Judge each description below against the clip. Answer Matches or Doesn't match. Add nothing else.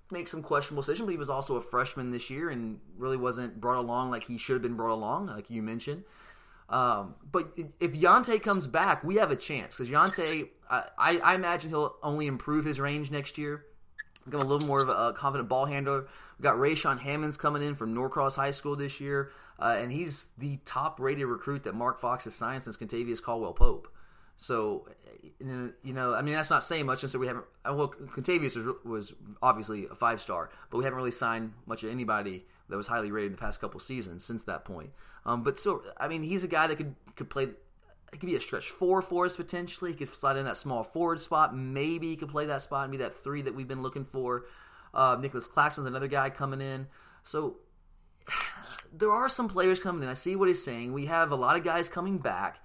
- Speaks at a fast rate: Matches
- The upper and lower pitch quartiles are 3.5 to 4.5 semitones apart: Matches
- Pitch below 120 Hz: Doesn't match